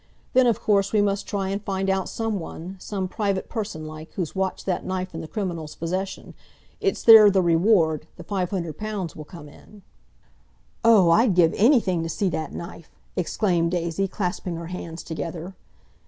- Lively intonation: No, average, 3.4 semitones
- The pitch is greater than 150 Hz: Yes, medium, 185 Hz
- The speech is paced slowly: No, average, 170 wpm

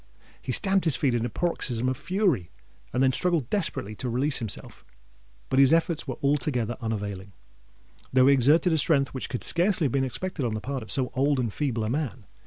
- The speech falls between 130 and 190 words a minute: No, average, 200 wpm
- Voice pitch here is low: Yes, low, 130 Hz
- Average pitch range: Yes, average, 4.6 semitones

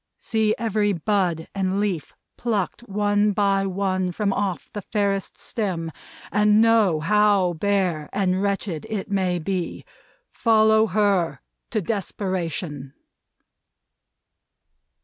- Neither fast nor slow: No, slow, 110 wpm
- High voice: Yes, high, 200 Hz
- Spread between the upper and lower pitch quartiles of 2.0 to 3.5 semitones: Yes, narrow, 2.5 semitones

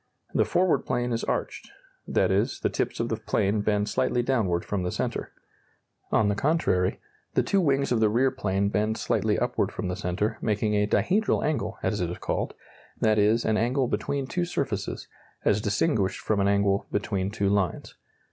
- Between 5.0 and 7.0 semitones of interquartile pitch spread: No, average, 3.8 semitones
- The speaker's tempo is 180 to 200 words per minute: Yes, average, 185 wpm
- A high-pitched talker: No, low, 105 Hz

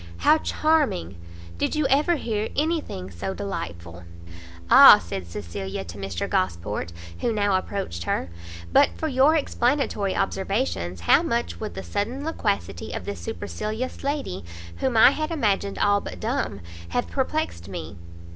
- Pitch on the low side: No, medium, 185 Hz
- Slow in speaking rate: No, average, 150 wpm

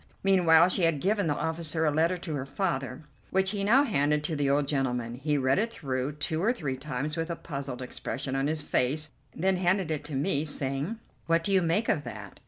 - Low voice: No, medium, 155 Hz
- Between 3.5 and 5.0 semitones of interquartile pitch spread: Yes, average, 4.3 semitones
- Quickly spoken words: Yes, fast, 220 wpm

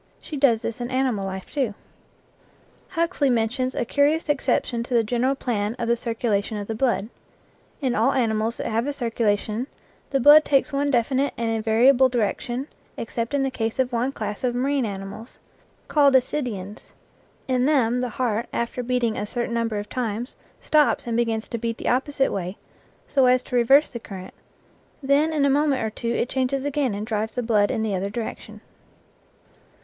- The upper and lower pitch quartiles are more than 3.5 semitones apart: No, average, 3.2 semitones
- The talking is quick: No, average, 180 wpm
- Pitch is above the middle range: Yes, high, 240 Hz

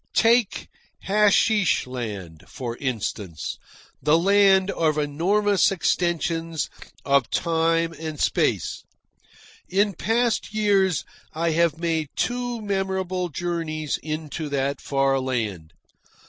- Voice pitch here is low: No, medium, 165 Hz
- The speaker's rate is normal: No, slow, 100 wpm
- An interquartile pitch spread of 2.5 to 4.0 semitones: No, wide, 5.5 semitones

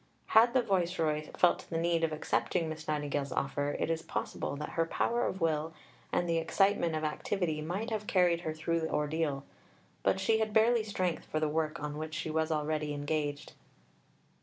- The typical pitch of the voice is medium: Yes, medium, 160 Hz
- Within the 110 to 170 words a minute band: No, average, 185 wpm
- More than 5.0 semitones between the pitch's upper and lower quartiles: No, average, 2.9 semitones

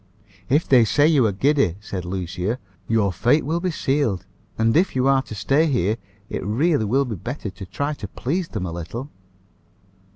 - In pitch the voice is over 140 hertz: No, low, 120 Hz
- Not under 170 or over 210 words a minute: Yes, average, 190 wpm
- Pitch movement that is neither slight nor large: No, wide, 6.6 semitones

